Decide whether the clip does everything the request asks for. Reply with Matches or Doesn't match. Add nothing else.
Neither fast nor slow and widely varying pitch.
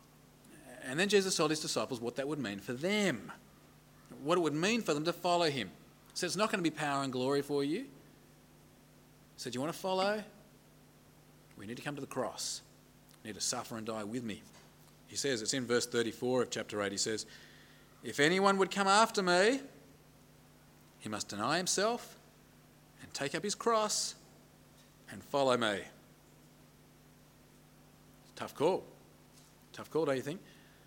Matches